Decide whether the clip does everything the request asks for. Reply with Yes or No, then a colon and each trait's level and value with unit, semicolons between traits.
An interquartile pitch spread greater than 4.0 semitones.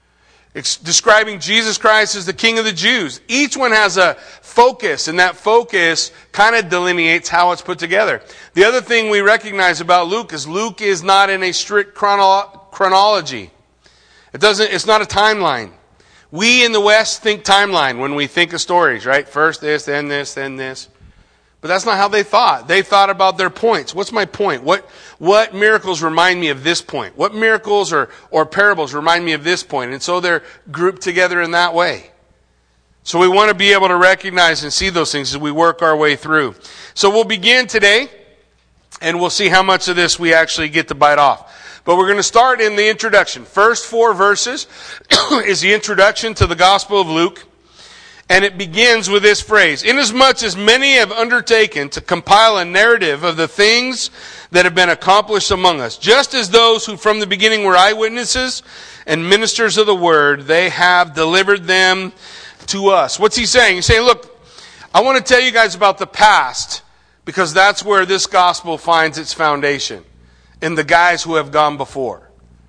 Yes: average, 4.6 semitones